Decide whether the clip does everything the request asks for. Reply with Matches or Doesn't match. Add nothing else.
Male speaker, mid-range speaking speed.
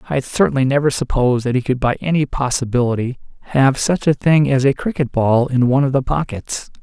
Doesn't match